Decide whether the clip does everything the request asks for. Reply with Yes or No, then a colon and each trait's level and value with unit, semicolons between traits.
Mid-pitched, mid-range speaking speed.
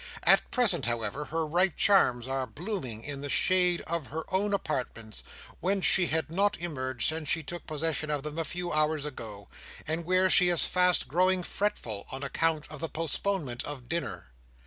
Yes: medium, 160 Hz; average, 180 wpm